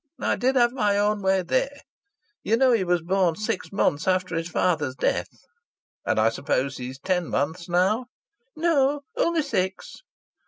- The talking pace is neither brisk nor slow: Yes, average, 160 wpm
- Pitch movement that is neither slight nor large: No, wide, 6.5 semitones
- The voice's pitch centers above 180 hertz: Yes, high, 190 Hz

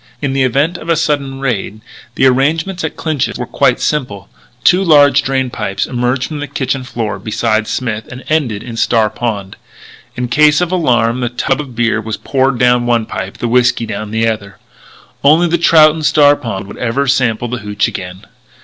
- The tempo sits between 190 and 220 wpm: Yes, average, 195 wpm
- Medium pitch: No, low, 125 Hz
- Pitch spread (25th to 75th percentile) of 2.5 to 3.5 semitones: No, average, 4.3 semitones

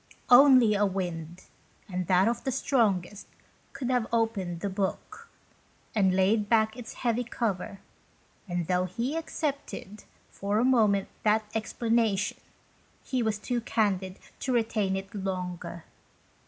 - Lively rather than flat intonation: No, average, 3.8 semitones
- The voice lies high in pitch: Yes, high, 210 Hz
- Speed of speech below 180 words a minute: Yes, slow, 135 wpm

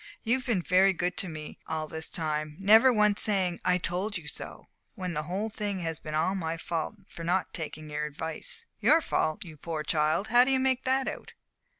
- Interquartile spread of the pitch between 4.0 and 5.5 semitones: Yes, average, 5.0 semitones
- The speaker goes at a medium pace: No, fast, 210 wpm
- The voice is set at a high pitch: No, medium, 180 Hz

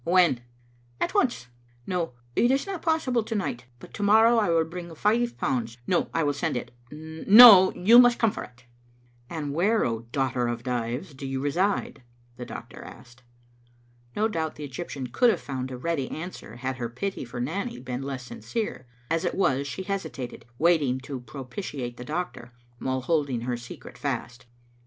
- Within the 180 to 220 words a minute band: Yes, average, 185 wpm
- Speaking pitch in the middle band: Yes, medium, 145 Hz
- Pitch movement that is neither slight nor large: No, wide, 7.6 semitones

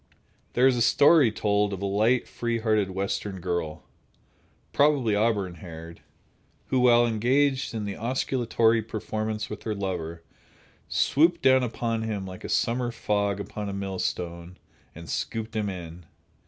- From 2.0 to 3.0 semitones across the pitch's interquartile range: No, average, 3.7 semitones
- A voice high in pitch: No, low, 105 Hz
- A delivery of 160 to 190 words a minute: No, average, 140 wpm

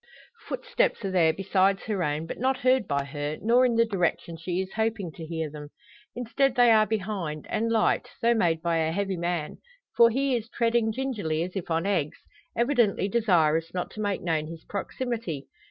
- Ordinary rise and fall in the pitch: No, wide, 5.9 semitones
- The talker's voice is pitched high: Yes, high, 195 Hz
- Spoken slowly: No, average, 190 wpm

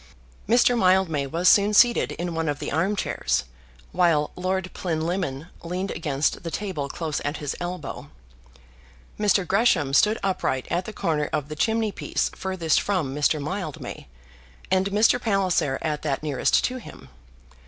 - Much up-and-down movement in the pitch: No, average, 4.6 semitones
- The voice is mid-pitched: Yes, medium, 175 Hz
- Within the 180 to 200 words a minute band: No, average, 150 wpm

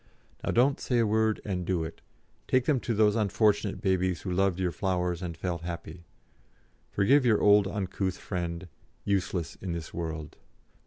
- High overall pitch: No, very low, 95 Hz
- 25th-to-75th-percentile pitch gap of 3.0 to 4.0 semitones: Yes, average, 3.3 semitones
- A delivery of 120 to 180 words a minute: Yes, average, 165 wpm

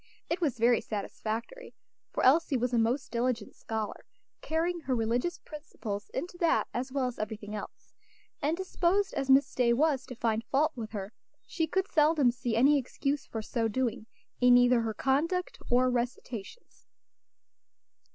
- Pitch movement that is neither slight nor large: Yes, average, 4.9 semitones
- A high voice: Yes, very high, 250 Hz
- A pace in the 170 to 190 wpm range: No, average, 160 wpm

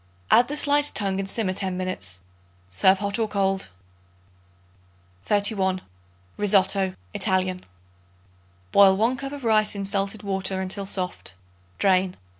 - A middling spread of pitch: No, narrow, 2.1 semitones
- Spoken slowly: Yes, slow, 125 wpm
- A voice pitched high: Yes, high, 195 Hz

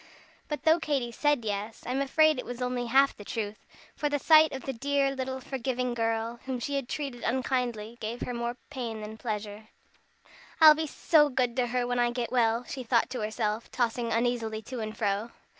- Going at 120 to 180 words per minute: No, fast, 205 wpm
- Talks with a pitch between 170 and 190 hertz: No, high, 245 Hz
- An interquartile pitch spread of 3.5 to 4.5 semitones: No, average, 2.9 semitones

